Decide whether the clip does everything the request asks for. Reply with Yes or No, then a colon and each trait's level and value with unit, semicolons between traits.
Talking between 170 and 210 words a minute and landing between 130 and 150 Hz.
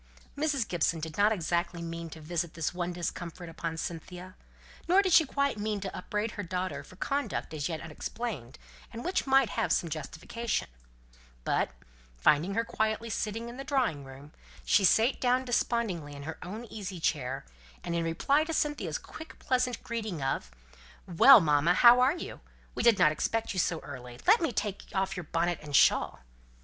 No: average, 180 wpm; medium, 185 Hz